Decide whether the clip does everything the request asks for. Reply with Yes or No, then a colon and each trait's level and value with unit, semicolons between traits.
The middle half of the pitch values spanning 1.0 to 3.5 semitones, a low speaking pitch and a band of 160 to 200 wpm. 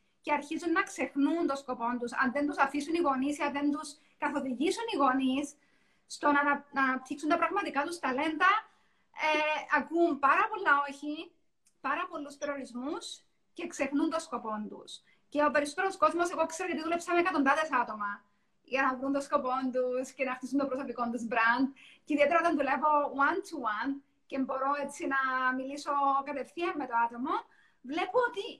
No: average, 3.2 semitones; very high, 285 Hz; fast, 170 wpm